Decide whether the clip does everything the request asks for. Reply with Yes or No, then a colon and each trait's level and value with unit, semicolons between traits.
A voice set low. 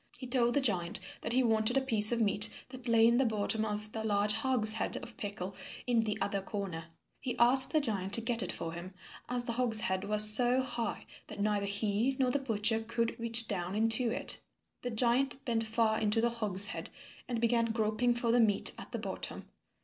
No: high, 225 Hz